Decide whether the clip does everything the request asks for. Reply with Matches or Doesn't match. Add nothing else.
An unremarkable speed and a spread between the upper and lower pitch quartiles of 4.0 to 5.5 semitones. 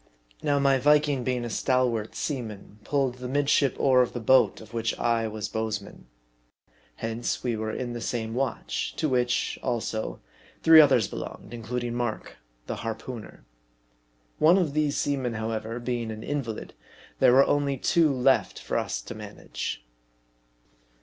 Doesn't match